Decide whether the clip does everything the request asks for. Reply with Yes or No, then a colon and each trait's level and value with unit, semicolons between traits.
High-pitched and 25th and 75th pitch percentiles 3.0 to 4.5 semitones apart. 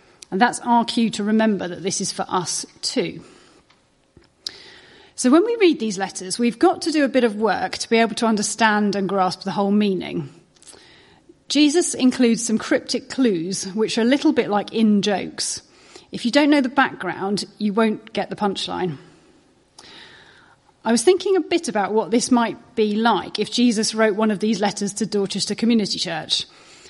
Yes: high, 220 Hz; average, 3.4 semitones